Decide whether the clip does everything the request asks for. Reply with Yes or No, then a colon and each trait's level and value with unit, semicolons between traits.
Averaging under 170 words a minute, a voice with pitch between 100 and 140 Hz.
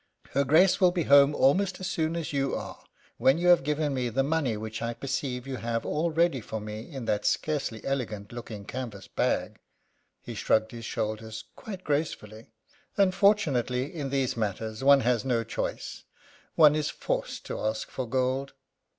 No: average, 175 wpm; low, 135 Hz